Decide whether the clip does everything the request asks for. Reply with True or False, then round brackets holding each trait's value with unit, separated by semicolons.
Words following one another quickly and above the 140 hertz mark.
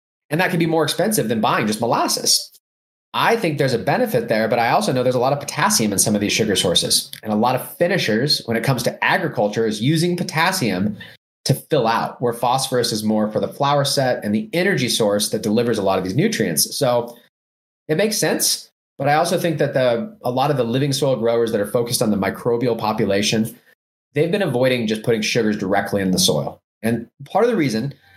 False (225 wpm; 120 Hz)